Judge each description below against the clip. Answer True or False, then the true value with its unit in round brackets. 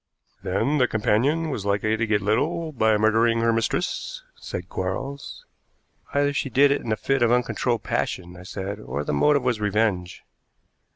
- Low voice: True (115 Hz)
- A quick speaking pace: False (170 wpm)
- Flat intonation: False (5.0 semitones)